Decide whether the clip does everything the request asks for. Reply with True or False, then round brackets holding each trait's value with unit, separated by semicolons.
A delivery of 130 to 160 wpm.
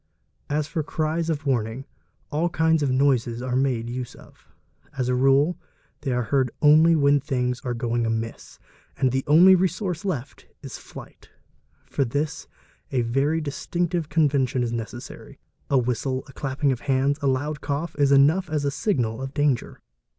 False (170 wpm)